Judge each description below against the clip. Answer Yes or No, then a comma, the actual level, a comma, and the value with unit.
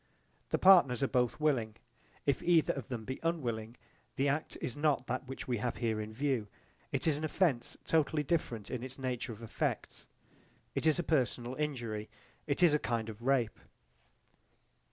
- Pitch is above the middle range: No, low, 130 Hz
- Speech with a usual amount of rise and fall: Yes, average, 4.2 semitones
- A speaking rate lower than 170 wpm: No, average, 175 wpm